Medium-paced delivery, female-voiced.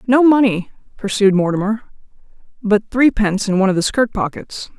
Yes: average, 150 wpm; female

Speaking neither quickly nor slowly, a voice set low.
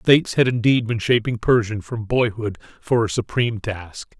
Yes: average, 185 wpm; low, 115 Hz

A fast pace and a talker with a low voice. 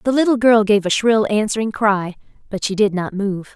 No: fast, 220 wpm; high, 210 Hz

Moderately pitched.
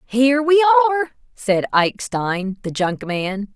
No: high, 240 Hz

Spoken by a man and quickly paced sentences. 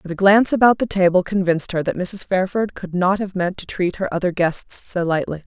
No: female; fast, 235 wpm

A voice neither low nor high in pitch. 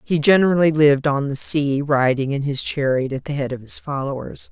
Yes: medium, 145 Hz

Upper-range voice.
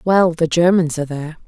No: medium, 165 Hz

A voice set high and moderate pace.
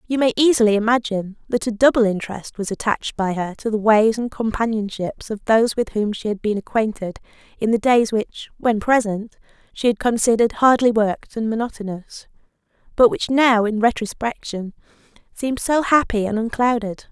Yes: high, 220 Hz; average, 170 wpm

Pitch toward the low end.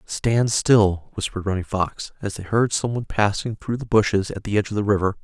Yes: low, 105 Hz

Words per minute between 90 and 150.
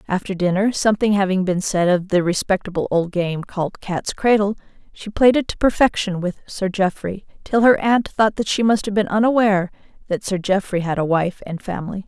No: average, 195 wpm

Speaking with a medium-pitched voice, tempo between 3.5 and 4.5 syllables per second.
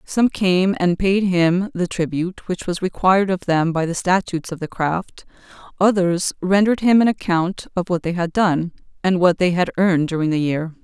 No: medium, 180 Hz; 5.0 syllables/s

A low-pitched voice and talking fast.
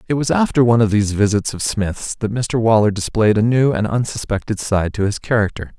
Yes: low, 110 Hz; fast, 220 wpm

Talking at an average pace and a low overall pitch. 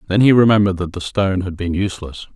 No: fast, 230 wpm; very low, 95 Hz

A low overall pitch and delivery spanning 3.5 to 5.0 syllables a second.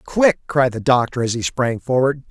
Yes: low, 130 Hz; 4.9 syllables/s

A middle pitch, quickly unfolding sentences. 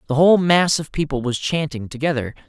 No: medium, 150 Hz; average, 195 wpm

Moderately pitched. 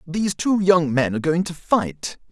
Yes: medium, 170 Hz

